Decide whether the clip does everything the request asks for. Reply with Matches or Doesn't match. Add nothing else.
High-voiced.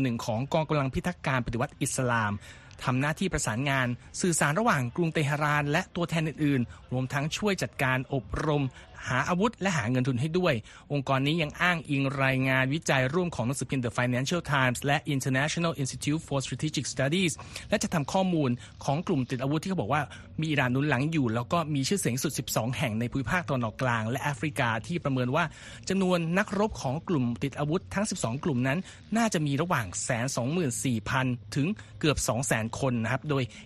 Doesn't match